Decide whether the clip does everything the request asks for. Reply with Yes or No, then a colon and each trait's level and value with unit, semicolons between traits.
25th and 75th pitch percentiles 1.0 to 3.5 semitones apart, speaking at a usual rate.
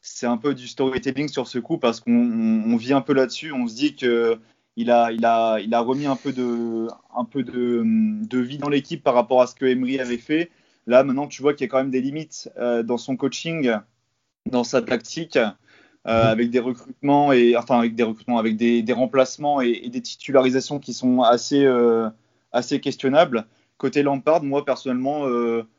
Yes: average, 2.9 semitones; average, 200 wpm